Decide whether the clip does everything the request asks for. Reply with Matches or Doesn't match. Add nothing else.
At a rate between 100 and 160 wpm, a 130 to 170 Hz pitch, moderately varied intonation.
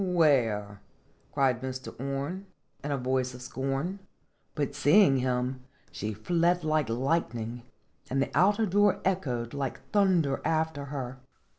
Matches